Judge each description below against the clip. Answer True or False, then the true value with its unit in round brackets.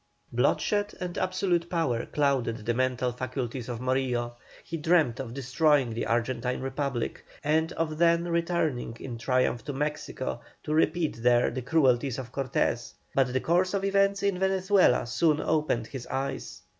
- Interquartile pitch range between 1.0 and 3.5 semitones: False (5.4 semitones)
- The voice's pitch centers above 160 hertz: False (135 Hz)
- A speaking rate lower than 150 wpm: False (155 wpm)